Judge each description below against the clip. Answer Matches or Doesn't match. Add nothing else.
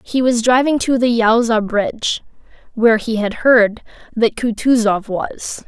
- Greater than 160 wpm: Doesn't match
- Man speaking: Doesn't match